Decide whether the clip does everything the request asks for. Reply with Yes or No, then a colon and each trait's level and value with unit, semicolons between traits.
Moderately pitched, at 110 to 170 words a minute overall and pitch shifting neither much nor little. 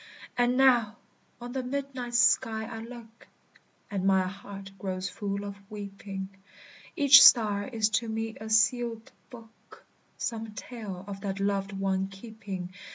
No: high, 215 Hz; average, 140 wpm; average, 3.3 semitones